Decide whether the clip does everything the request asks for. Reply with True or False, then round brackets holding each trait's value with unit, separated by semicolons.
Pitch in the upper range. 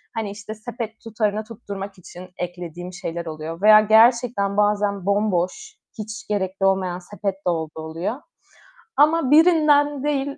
True (205 Hz)